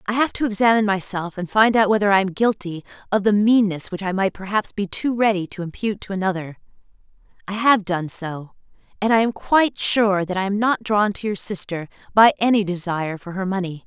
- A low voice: No, high, 200 Hz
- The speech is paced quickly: Yes, fast, 210 wpm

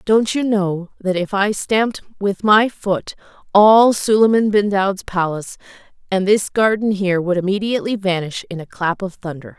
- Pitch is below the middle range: No, high, 200 Hz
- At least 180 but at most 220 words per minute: No, average, 170 wpm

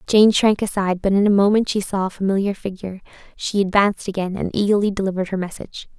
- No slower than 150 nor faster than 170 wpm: No, average, 200 wpm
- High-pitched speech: Yes, high, 195 Hz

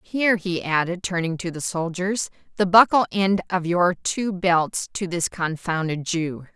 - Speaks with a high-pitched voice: No, medium, 180 Hz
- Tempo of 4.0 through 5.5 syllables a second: Yes, 4.3 syllables/s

